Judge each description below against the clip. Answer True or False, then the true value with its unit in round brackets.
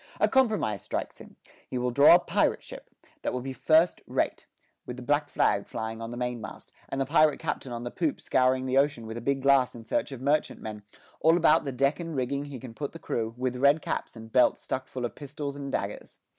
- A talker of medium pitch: False (130 Hz)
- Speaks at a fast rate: True (230 wpm)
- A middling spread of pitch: True (3.0 semitones)